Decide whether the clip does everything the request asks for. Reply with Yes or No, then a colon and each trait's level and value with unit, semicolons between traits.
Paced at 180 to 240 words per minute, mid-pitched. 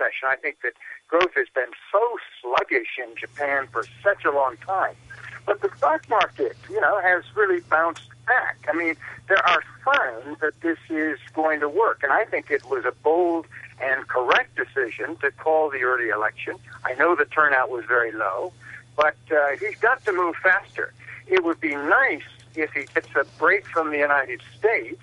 Yes: average, 185 wpm; medium, 160 Hz